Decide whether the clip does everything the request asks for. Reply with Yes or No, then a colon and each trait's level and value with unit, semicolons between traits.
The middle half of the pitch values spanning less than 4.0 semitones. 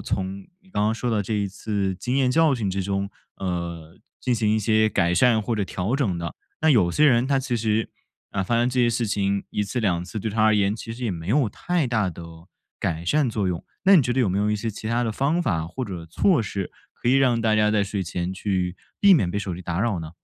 No: average, 4.3 semitones